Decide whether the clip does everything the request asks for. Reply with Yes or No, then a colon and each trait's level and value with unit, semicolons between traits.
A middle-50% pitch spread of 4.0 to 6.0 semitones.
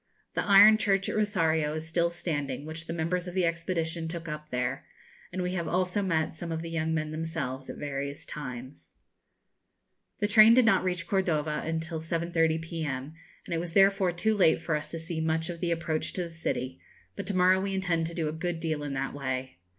No: narrow, 2.6 semitones